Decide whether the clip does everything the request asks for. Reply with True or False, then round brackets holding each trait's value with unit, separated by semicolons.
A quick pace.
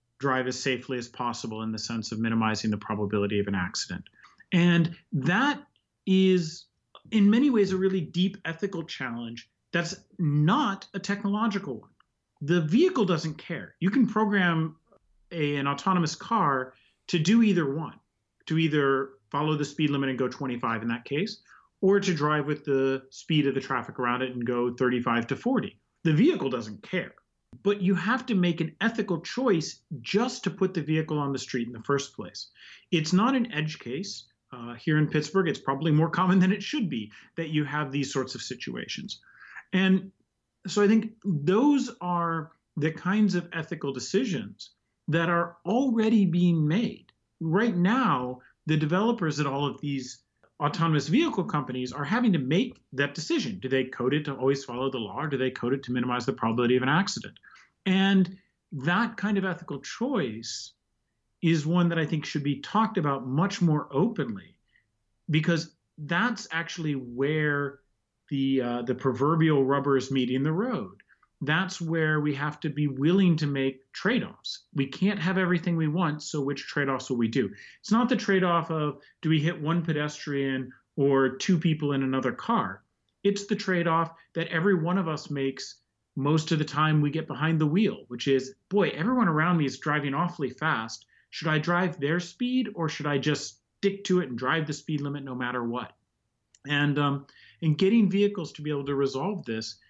False (185 wpm)